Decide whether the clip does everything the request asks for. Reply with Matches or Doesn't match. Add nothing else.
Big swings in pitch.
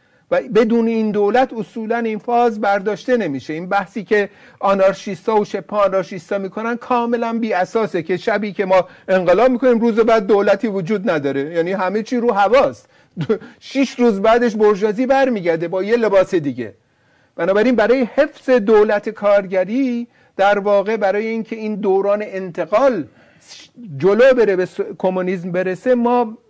Doesn't match